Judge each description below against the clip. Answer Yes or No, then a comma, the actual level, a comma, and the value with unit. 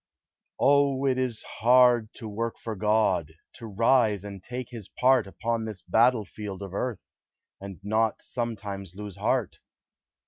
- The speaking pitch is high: No, low, 110 Hz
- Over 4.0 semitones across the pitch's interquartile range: No, average, 3.5 semitones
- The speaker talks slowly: No, average, 145 wpm